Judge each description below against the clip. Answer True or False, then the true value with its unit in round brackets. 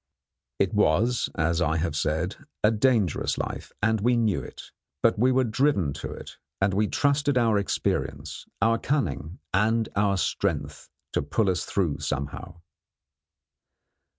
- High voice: False (105 Hz)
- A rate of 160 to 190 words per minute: False (150 wpm)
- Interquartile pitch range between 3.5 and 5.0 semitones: False (5.4 semitones)